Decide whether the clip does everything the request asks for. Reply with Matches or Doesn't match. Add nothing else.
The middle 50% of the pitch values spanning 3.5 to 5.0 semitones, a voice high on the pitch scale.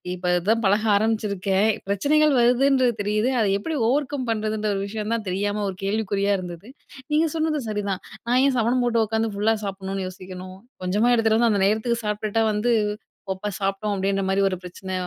Doesn't match